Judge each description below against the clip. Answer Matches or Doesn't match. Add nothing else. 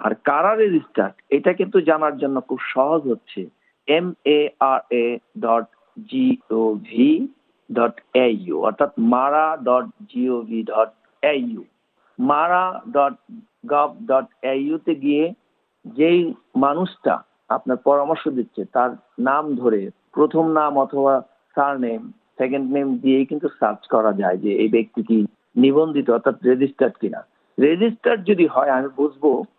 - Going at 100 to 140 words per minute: Matches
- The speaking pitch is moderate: Matches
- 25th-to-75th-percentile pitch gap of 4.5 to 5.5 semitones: Matches